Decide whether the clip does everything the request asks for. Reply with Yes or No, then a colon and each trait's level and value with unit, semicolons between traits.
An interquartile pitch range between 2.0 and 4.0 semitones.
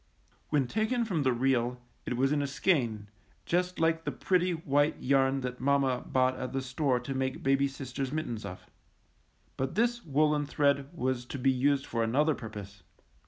Yes: average, 3.1 semitones